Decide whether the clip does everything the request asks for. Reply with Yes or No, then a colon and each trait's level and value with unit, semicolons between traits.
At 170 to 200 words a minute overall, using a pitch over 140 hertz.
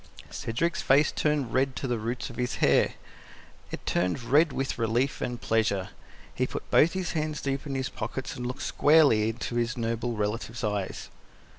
No: average, 175 wpm; low, 125 Hz